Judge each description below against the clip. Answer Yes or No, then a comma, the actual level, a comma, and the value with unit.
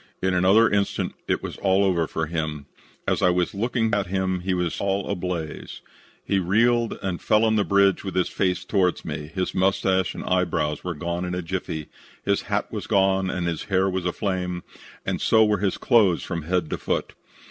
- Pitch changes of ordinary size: No, narrow, 2.1 semitones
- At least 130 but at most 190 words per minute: No, average, 200 wpm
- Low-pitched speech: Yes, very low, 95 Hz